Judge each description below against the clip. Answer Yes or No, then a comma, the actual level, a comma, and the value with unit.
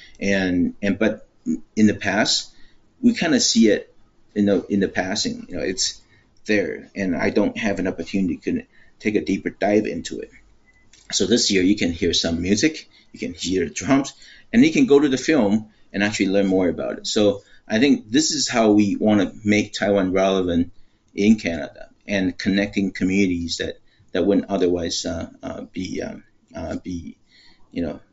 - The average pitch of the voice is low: Yes, low, 105 Hz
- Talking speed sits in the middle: Yes, average, 185 wpm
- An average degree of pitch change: Yes, average, 3.1 semitones